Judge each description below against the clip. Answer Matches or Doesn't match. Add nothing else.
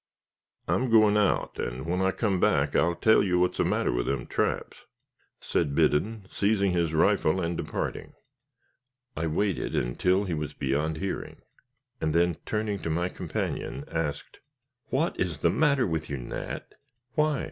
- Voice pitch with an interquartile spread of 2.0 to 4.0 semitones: Doesn't match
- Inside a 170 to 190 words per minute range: Doesn't match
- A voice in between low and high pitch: Doesn't match